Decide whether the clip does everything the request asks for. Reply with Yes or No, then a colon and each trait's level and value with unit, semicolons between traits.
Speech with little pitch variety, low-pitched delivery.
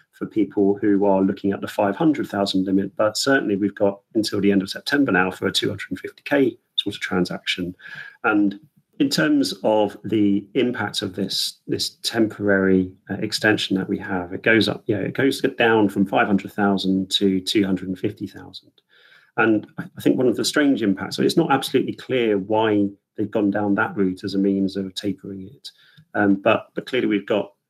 Yes: narrow, 1.8 semitones; low, 100 Hz